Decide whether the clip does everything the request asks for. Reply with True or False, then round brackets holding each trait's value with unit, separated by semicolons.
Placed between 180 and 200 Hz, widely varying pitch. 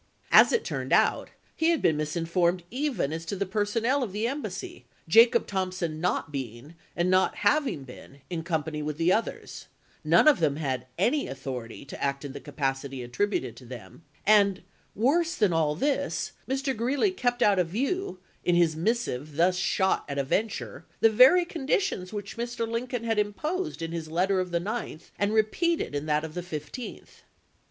True (185 Hz; 7.5 semitones)